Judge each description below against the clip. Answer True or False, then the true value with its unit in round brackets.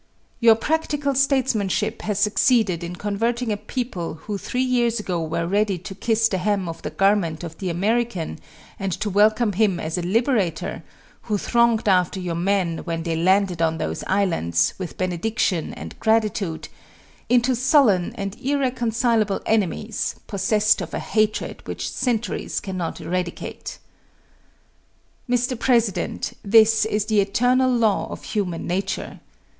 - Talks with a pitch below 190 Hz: False (205 Hz)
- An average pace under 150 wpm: True (140 wpm)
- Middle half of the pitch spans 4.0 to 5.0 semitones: True (4.3 semitones)